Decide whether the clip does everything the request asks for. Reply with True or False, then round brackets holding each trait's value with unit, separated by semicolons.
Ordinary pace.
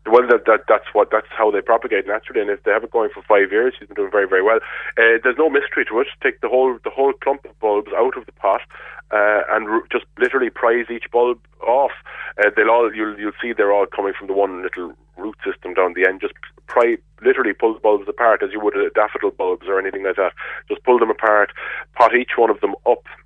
False (245 wpm)